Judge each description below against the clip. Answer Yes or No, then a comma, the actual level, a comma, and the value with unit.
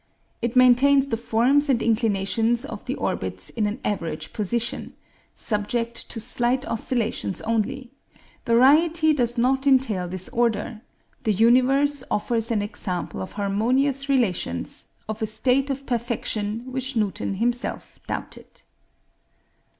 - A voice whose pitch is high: Yes, high, 235 Hz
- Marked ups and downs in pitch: No, average, 3.5 semitones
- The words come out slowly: Yes, slow, 120 wpm